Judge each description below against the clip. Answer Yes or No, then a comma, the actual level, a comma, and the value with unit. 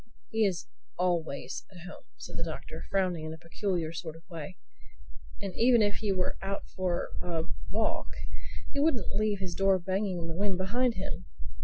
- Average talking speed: Yes, average, 180 wpm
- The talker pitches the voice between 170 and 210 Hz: Yes, medium, 185 Hz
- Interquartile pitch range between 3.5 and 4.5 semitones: No, average, 3.1 semitones